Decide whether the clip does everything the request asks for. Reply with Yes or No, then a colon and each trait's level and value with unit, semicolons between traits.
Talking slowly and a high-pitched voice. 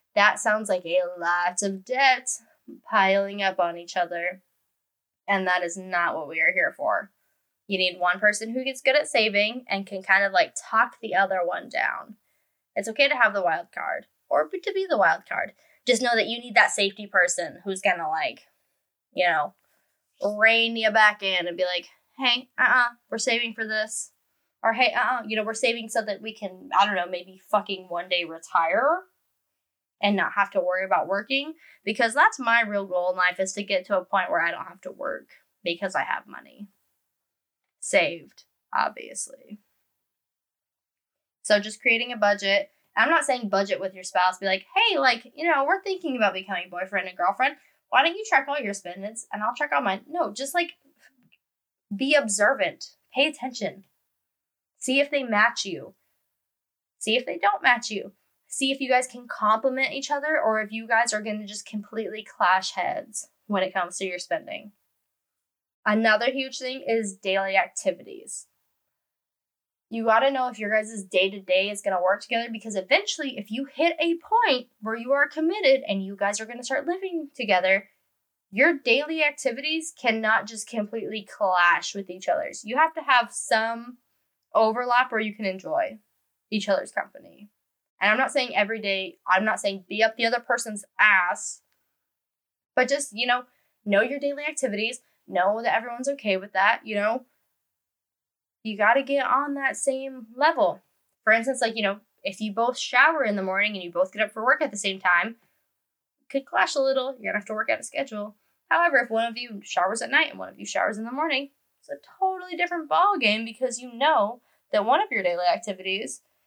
No: average, 195 wpm; high, 225 Hz